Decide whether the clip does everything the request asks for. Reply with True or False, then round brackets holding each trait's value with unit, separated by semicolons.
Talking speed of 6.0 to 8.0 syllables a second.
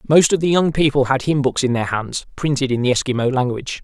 True (6.2 syllables/s)